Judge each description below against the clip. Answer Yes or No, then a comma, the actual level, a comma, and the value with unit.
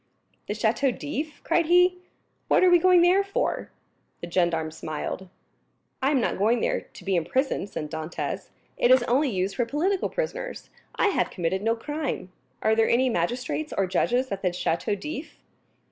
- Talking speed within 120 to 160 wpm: No, average, 175 wpm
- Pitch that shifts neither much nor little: No, wide, 8.6 semitones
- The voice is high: Yes, high, 245 Hz